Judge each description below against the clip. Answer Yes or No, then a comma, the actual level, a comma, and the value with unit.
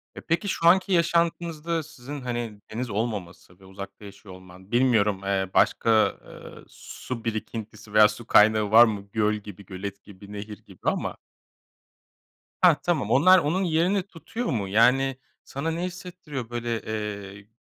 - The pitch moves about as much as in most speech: No, wide, 7.4 semitones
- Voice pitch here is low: Yes, low, 115 Hz